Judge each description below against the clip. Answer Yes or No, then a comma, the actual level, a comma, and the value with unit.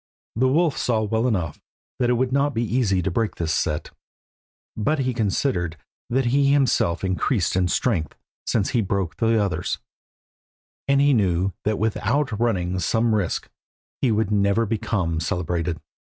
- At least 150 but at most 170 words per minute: Yes, average, 160 wpm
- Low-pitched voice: Yes, low, 110 Hz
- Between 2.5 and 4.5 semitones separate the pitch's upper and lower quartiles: No, average, 5.3 semitones